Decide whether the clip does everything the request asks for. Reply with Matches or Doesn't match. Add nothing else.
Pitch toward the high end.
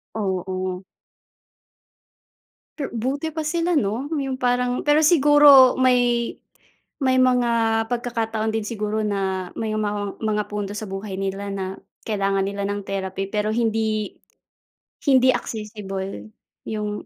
Matches